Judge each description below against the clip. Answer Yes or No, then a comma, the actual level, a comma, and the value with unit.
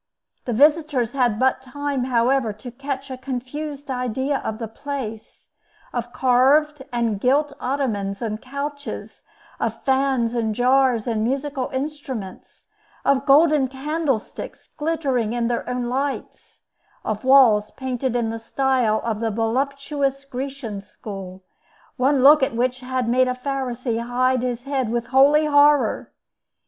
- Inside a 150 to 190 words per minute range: No, slow, 135 wpm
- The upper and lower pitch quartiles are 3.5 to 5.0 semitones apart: No, average, 2.9 semitones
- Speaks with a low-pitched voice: No, very high, 255 Hz